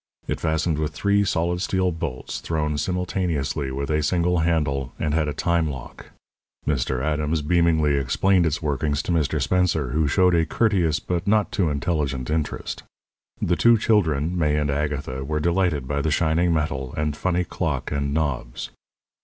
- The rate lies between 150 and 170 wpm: Yes, average, 165 wpm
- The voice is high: No, very low, 80 Hz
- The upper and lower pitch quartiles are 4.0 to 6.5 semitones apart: No, average, 3.1 semitones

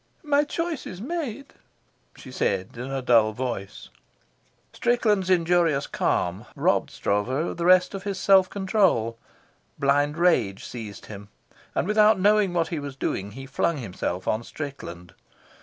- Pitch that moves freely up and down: Yes, wide, 9.0 semitones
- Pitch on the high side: No, medium, 150 Hz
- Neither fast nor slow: Yes, average, 145 wpm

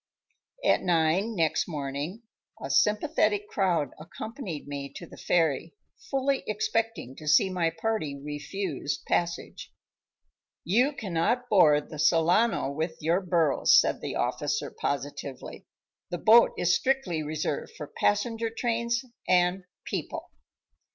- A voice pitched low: No, medium, 175 Hz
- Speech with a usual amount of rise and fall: No, wide, 6.1 semitones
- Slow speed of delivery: Yes, slow, 120 wpm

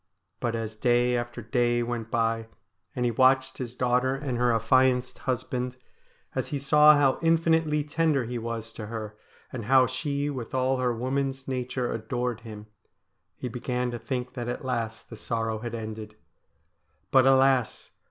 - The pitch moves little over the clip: Yes, narrow, 2.3 semitones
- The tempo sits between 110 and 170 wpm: Yes, average, 160 wpm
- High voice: No, low, 125 Hz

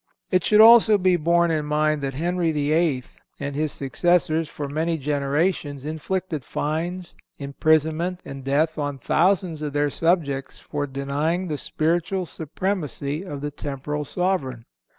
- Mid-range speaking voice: Yes, medium, 155 Hz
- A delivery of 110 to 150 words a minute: Yes, average, 140 wpm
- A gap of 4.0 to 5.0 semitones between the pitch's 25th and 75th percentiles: No, average, 3.3 semitones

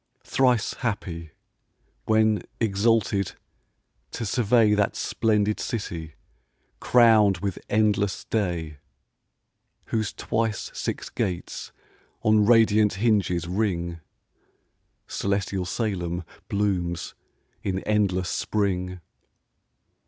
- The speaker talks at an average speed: No, slow, 80 wpm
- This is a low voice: Yes, low, 100 Hz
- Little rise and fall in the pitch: No, average, 3.2 semitones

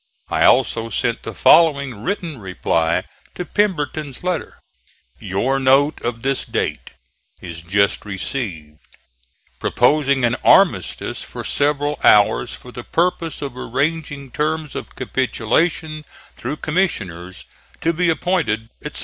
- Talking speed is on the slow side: Yes, slow, 120 wpm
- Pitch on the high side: No, low, 135 Hz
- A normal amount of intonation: No, wide, 5.8 semitones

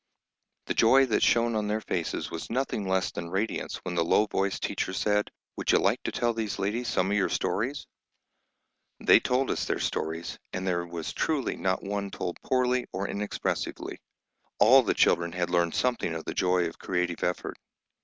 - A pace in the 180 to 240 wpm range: Yes, average, 185 wpm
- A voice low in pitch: Yes, low, 100 Hz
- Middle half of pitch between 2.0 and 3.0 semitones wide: No, average, 4.7 semitones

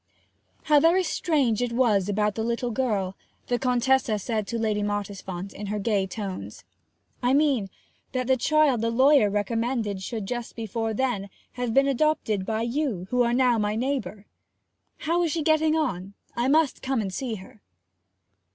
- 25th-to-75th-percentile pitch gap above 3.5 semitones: Yes, average, 4.3 semitones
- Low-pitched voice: No, high, 235 Hz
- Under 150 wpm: No, average, 170 wpm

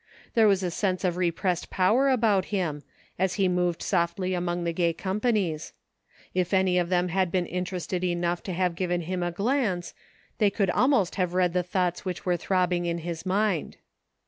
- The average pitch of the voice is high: No, medium, 180 Hz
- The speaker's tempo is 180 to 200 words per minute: Yes, average, 185 wpm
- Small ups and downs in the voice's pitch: Yes, narrow, 1.6 semitones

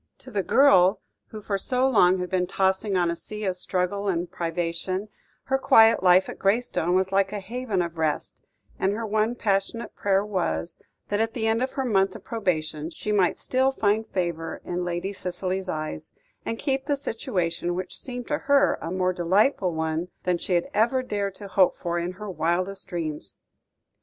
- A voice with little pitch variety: No, average, 3.8 semitones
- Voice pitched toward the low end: No, high, 190 Hz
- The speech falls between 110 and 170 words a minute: No, average, 190 wpm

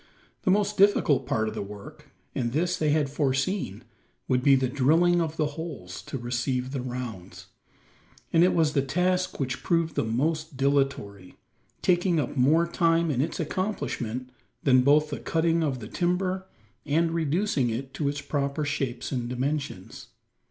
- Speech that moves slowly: No, average, 165 wpm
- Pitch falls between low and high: Yes, medium, 145 Hz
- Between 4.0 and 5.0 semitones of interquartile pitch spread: Yes, average, 4.7 semitones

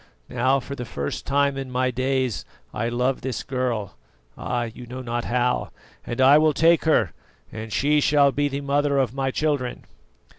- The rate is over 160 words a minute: Yes, average, 180 wpm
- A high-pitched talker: No, low, 130 Hz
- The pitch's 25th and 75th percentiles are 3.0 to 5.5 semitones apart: No, narrow, 2.4 semitones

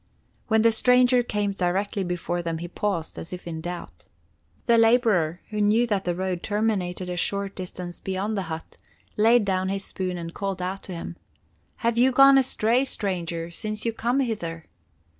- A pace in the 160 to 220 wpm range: Yes, average, 180 wpm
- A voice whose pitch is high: Yes, high, 195 Hz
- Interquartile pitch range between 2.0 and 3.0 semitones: No, average, 4.1 semitones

